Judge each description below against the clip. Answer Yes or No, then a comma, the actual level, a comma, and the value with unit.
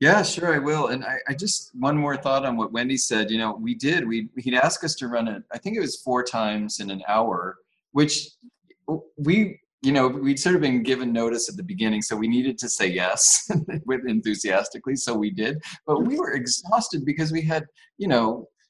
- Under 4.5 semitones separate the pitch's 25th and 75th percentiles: No, wide, 5.6 semitones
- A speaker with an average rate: No, fast, 220 wpm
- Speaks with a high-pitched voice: No, low, 135 Hz